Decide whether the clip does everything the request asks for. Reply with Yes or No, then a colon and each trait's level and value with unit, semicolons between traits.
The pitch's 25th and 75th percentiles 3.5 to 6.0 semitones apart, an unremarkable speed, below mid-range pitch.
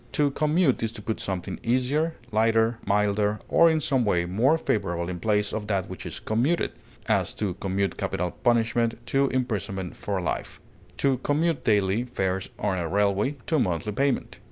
Yes: average, 5.1 semitones; average, 175 wpm; low, 110 Hz